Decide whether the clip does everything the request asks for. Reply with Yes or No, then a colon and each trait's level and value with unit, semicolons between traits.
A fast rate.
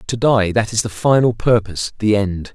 Yes: fast, 215 wpm